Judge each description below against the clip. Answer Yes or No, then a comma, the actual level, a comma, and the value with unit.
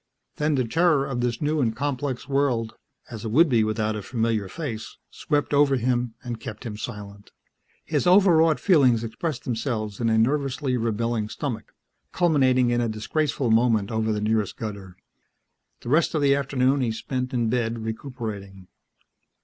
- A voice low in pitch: Yes, low, 120 Hz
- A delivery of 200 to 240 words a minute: No, average, 165 wpm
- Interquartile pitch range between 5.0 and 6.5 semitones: No, average, 4.0 semitones